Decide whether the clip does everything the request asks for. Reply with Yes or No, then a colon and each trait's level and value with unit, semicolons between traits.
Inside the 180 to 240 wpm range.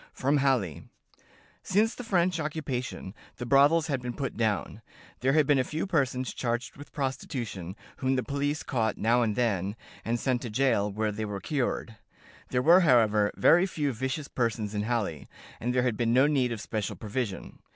Yes: average, 185 wpm